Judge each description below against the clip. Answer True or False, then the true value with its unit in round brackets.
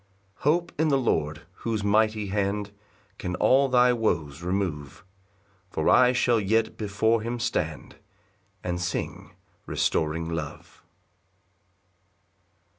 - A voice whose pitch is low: True (105 Hz)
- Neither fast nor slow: False (115 wpm)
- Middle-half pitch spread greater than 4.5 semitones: True (5.4 semitones)